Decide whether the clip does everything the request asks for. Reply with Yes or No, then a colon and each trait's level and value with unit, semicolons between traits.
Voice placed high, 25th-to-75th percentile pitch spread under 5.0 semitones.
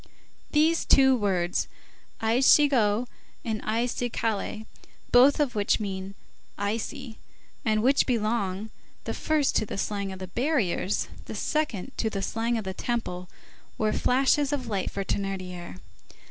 Yes: high, 220 Hz; average, 4.6 semitones